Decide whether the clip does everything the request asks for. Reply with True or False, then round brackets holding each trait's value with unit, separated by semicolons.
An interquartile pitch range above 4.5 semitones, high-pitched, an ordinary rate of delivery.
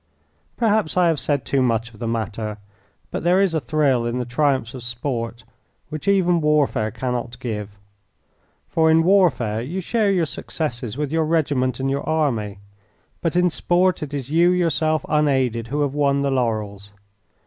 False (5.5 semitones; 140 Hz; 170 wpm)